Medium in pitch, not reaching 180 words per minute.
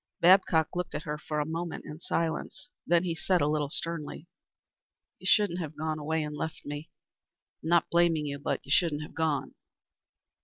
No: medium, 160 Hz; average, 185 wpm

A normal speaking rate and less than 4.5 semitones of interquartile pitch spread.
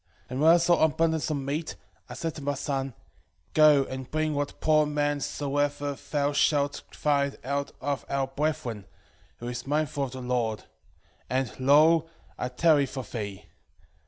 Yes: average, 165 wpm; narrow, 2.5 semitones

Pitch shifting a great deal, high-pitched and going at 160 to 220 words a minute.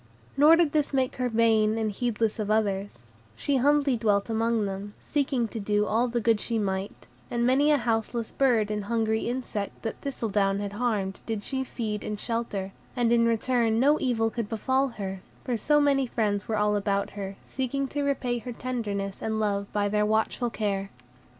No: average, 3.2 semitones; high, 225 Hz; average, 190 wpm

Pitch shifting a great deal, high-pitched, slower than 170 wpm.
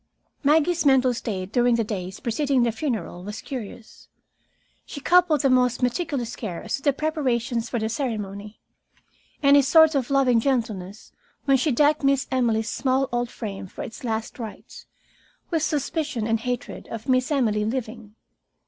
No: average, 3.9 semitones; high, 245 Hz; average, 160 wpm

